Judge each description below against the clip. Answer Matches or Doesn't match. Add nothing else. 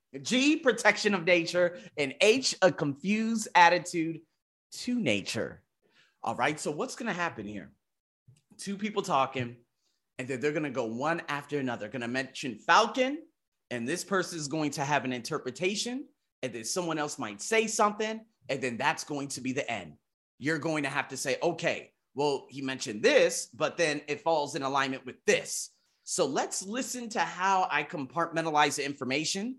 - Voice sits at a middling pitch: Matches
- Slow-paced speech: Doesn't match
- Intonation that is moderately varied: Doesn't match